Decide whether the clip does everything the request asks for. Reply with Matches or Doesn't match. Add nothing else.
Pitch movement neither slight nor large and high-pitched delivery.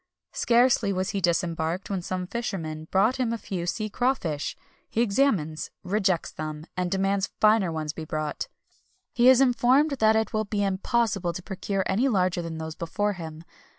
Matches